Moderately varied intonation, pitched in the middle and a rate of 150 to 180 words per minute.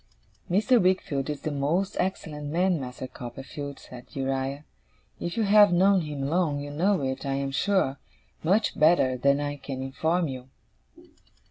Yes: average, 4.9 semitones; medium, 145 Hz; average, 155 wpm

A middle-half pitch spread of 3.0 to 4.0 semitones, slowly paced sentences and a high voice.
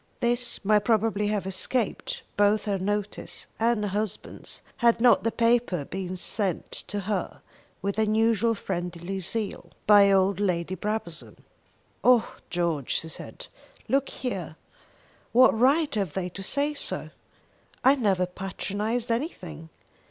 Yes: average, 3.6 semitones; slow, 130 wpm; high, 205 Hz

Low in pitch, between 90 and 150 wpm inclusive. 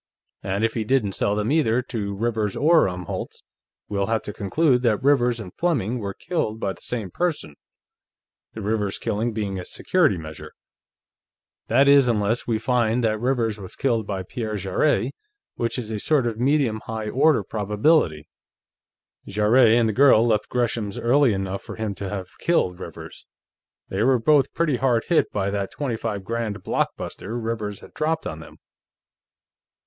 No: low, 110 Hz; average, 170 wpm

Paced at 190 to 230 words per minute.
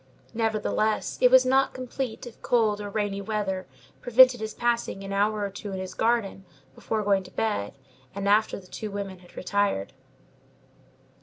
No: average, 165 wpm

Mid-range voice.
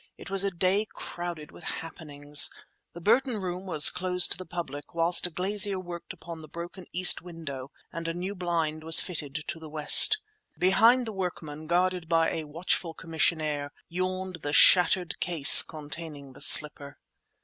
Yes: medium, 170 Hz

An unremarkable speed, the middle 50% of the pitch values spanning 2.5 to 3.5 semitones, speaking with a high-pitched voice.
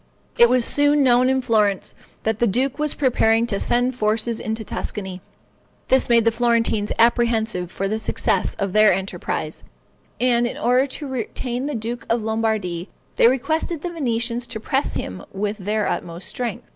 Yes: average, 170 wpm; average, 2.8 semitones; high, 230 Hz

